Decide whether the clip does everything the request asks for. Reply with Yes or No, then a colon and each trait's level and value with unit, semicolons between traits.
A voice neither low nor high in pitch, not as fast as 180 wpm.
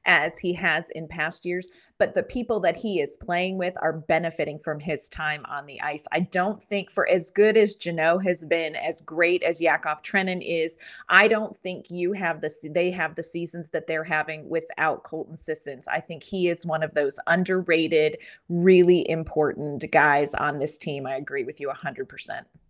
No: medium, 165 Hz; average, 200 wpm